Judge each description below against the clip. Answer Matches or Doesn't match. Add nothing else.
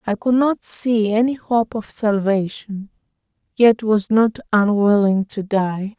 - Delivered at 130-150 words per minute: Matches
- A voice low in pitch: Doesn't match